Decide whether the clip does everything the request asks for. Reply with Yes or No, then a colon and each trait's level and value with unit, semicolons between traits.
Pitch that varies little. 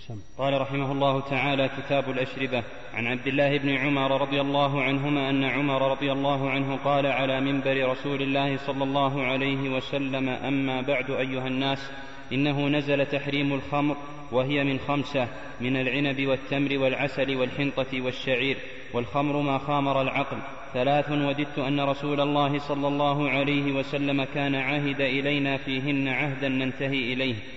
Yes: narrow, 1.2 semitones